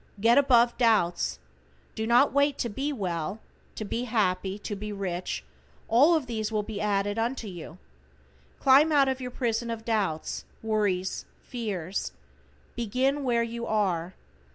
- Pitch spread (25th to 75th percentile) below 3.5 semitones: No, average, 3.8 semitones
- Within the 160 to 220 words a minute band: No, average, 150 wpm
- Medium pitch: No, high, 225 Hz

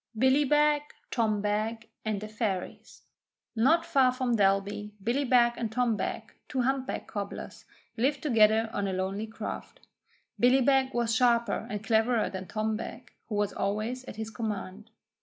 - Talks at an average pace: Yes, average, 160 wpm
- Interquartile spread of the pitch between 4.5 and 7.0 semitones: No, average, 3.3 semitones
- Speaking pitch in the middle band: No, high, 225 Hz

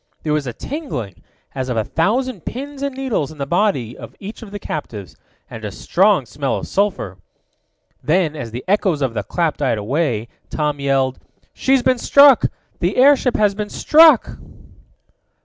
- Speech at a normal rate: Yes, average, 170 wpm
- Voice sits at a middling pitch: Yes, medium, 165 Hz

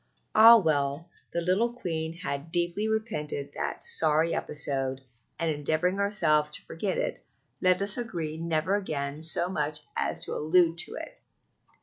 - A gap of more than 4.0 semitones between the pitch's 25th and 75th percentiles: No, average, 3.7 semitones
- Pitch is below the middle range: No, medium, 165 Hz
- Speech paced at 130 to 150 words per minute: Yes, average, 145 wpm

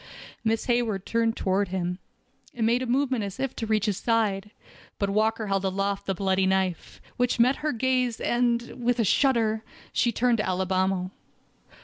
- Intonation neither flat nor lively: Yes, average, 3.8 semitones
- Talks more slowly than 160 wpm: No, average, 170 wpm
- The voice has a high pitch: Yes, high, 220 Hz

